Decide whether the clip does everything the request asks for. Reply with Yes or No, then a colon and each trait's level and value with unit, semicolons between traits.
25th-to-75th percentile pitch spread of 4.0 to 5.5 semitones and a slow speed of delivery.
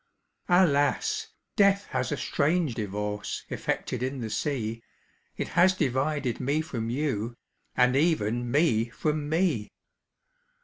Yes: average, 5.2 semitones; slow, 120 wpm